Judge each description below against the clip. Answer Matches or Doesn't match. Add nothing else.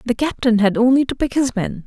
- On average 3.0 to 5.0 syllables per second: Doesn't match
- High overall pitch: Matches